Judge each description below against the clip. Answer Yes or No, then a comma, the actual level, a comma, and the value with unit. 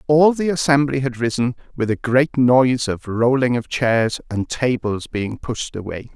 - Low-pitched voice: Yes, low, 125 Hz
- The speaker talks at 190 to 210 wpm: No, average, 175 wpm